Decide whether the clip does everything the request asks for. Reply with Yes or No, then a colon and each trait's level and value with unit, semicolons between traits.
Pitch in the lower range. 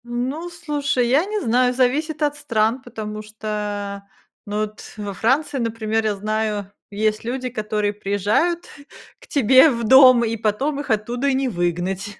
No: high, 230 Hz